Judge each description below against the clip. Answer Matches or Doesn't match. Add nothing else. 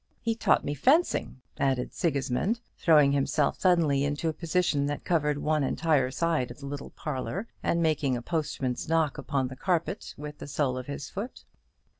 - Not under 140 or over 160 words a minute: Doesn't match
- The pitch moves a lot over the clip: Doesn't match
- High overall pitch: Doesn't match